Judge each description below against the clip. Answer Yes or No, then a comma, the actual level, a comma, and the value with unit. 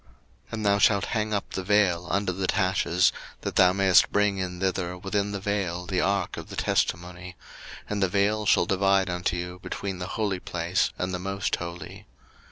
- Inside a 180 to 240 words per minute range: Yes, average, 190 wpm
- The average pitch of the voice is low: Yes, very low, 95 Hz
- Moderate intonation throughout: No, narrow, 2.0 semitones